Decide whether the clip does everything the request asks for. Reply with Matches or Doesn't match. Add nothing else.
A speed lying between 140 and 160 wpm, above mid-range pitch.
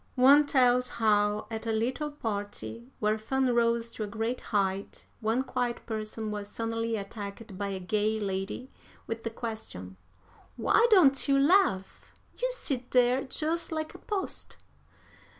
Matches